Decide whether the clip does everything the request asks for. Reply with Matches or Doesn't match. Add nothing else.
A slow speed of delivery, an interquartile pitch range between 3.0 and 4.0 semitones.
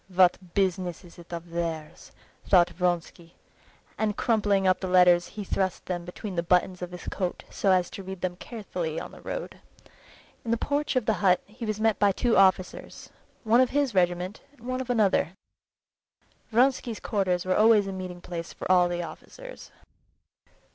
Doesn't match